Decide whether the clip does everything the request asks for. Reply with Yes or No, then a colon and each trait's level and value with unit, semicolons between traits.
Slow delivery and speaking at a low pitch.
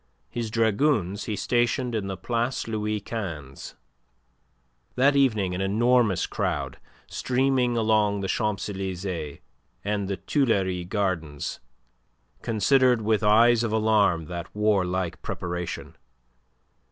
Yes: slow, 110 wpm; low, 105 Hz